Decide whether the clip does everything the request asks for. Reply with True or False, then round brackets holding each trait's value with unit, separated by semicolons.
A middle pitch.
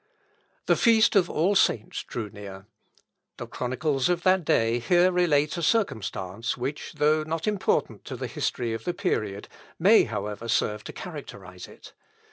True (145 Hz)